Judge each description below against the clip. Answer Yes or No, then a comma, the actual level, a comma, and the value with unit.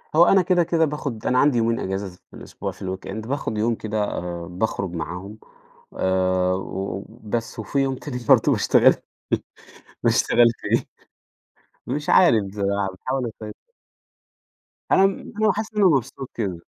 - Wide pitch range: Yes, wide, 6.3 semitones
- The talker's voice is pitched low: Yes, low, 110 Hz